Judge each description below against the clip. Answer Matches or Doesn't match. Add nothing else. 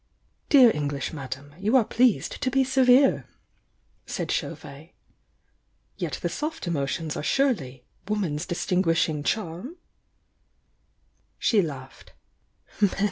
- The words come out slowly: Matches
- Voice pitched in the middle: Matches